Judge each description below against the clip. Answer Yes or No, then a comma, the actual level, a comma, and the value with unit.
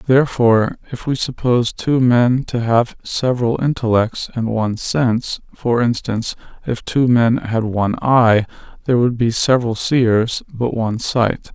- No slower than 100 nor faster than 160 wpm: Yes, average, 140 wpm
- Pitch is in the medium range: No, low, 120 Hz